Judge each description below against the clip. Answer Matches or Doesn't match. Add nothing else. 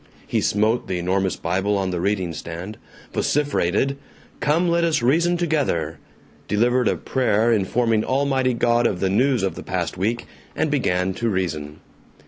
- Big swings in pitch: Matches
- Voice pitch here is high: Doesn't match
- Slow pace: Doesn't match